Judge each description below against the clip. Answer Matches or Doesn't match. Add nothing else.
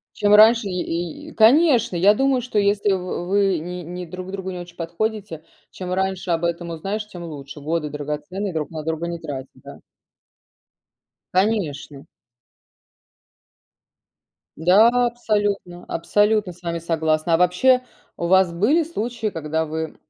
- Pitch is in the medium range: Matches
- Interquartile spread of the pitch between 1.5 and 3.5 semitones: Doesn't match